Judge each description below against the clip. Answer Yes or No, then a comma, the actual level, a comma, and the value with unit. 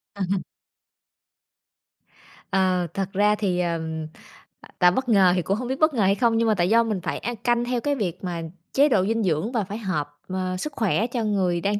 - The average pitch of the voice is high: Yes, high, 200 Hz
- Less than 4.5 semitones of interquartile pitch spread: Yes, average, 4.1 semitones